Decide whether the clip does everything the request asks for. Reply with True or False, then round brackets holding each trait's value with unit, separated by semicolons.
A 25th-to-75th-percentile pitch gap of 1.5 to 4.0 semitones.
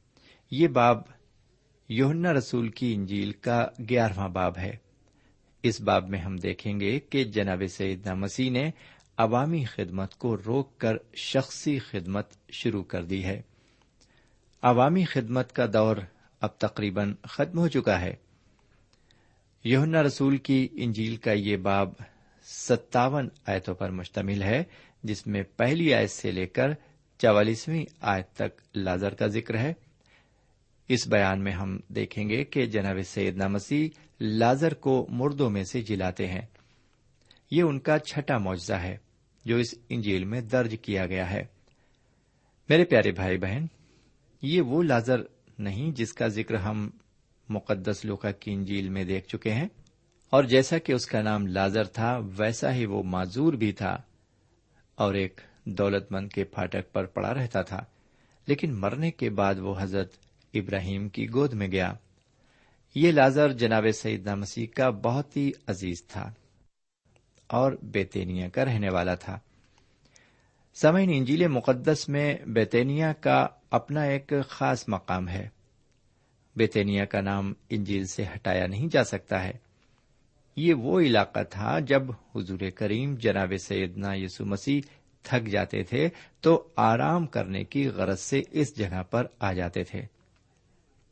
False (4.9 semitones)